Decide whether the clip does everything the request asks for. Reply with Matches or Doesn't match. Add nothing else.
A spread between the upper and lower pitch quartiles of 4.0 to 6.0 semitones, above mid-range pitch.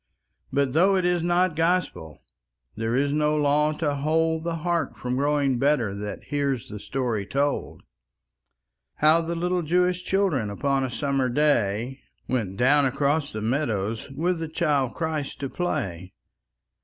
Doesn't match